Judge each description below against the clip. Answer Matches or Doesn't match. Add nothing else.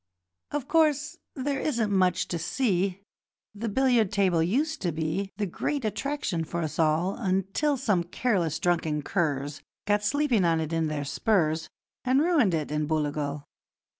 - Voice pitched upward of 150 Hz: Matches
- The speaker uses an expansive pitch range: Matches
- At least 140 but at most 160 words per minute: Matches